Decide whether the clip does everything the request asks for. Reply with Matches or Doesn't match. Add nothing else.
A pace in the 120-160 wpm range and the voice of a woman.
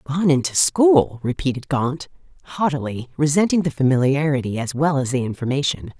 Matches